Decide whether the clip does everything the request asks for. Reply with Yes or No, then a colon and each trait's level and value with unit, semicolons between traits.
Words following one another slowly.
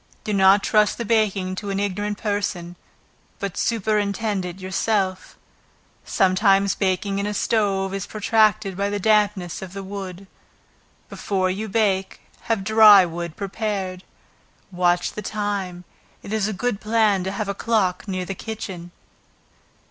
No: average, 145 wpm